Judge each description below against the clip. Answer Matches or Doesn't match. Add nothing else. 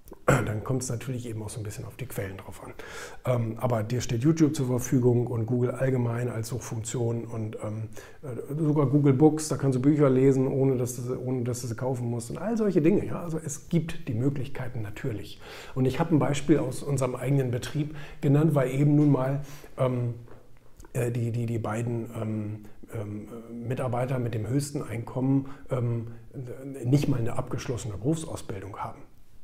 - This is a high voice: Doesn't match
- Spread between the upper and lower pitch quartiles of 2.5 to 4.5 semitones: Matches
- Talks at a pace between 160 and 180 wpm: Matches